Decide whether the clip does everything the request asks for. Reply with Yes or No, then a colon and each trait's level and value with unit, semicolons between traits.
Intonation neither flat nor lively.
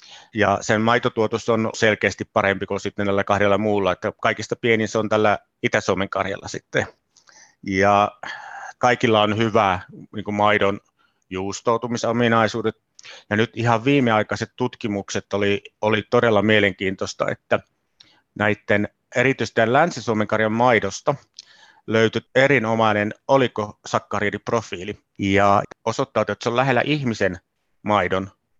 No: narrow, 2.3 semitones